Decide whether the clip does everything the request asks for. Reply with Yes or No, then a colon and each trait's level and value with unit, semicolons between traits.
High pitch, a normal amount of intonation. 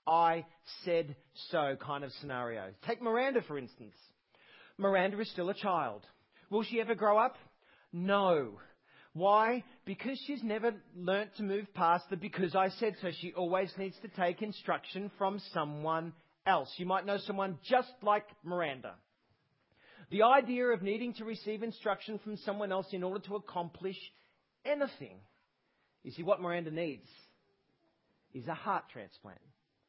Yes: high, 195 Hz; average, 4.0 semitones